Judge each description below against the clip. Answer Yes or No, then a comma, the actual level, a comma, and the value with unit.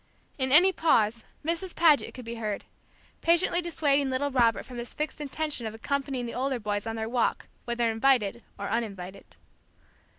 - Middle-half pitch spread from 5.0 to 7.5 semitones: No, average, 4.4 semitones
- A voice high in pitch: Yes, very high, 250 Hz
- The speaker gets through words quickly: No, average, 165 wpm